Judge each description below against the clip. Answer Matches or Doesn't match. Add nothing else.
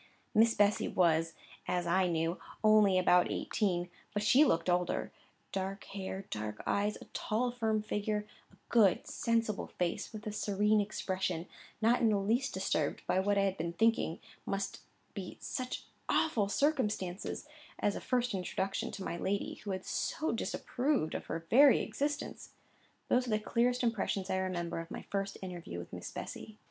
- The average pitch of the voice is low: Doesn't match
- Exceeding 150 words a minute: Matches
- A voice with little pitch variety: Doesn't match